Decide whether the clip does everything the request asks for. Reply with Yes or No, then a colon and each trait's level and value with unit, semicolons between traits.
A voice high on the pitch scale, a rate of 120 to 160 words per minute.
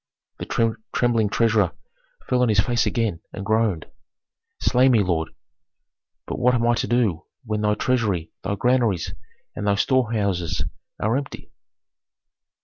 No: low, 110 Hz; average, 140 wpm